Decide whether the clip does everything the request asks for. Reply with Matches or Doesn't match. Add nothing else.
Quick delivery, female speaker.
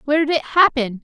Matches